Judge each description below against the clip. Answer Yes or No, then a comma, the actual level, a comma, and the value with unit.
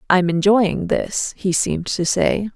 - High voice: Yes, high, 195 Hz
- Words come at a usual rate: Yes, average, 165 wpm